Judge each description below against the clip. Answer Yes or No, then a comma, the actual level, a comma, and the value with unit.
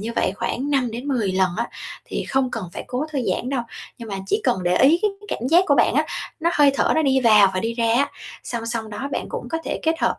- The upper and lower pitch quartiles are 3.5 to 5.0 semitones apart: Yes, average, 3.9 semitones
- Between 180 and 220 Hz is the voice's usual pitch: No, high, 245 Hz